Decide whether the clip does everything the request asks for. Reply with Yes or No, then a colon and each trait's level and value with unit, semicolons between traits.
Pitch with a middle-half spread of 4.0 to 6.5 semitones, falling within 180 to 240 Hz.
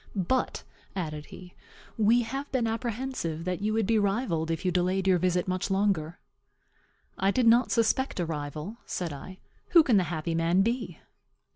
Yes: average, 5.0 semitones; high, 190 Hz